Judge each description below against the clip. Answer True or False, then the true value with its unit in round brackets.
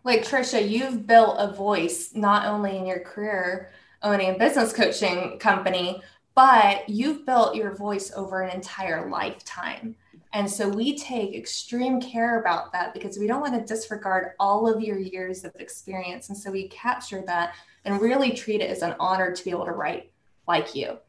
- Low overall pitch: False (205 Hz)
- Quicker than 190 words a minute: False (180 wpm)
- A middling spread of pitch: True (3.4 semitones)